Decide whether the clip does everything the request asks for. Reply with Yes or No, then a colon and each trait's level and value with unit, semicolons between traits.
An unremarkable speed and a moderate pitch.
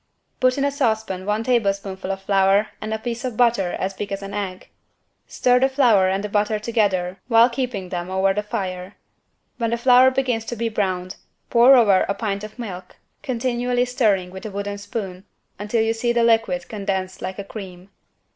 No: average, 195 wpm; high, 210 Hz